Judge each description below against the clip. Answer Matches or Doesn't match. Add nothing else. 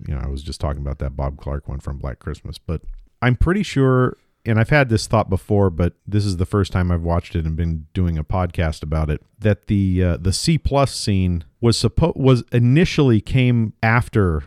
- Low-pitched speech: Matches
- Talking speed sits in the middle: Doesn't match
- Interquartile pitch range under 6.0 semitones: Doesn't match